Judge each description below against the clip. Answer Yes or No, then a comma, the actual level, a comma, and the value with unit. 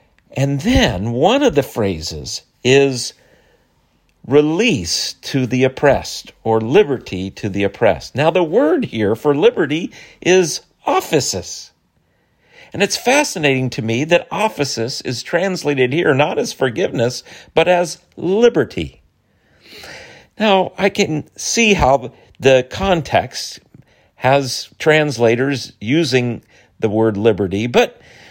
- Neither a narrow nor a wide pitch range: No, wide, 6.9 semitones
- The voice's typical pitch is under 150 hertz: Yes, low, 135 Hz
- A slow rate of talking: Yes, slow, 115 wpm